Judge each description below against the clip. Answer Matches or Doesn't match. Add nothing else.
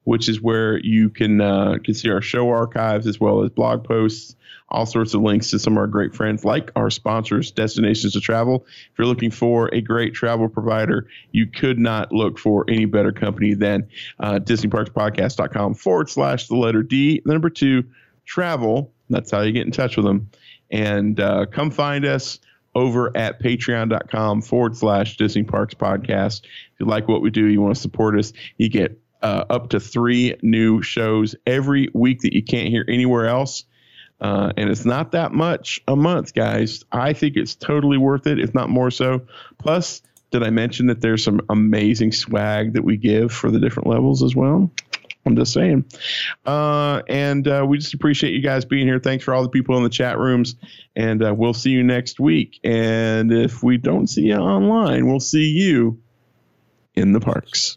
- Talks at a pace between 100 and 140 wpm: Doesn't match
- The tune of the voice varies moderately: Matches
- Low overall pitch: Matches